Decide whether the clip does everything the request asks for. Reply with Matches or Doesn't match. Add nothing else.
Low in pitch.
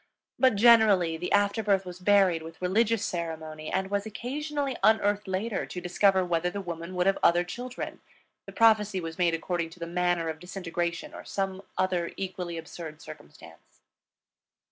Doesn't match